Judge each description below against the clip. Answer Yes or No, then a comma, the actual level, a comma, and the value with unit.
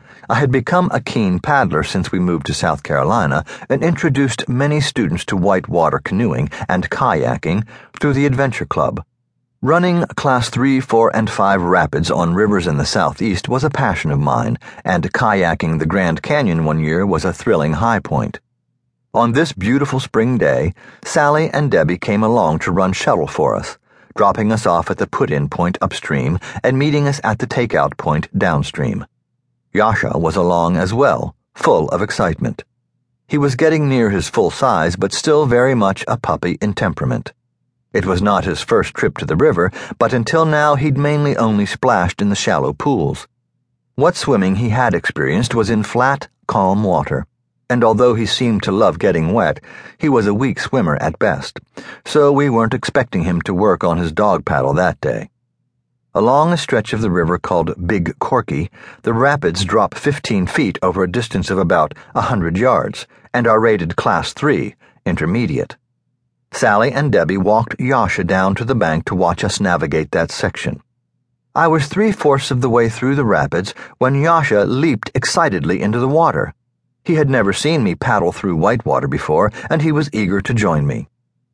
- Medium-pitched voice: No, low, 125 Hz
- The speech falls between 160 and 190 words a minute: Yes, average, 180 wpm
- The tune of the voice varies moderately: No, wide, 6.4 semitones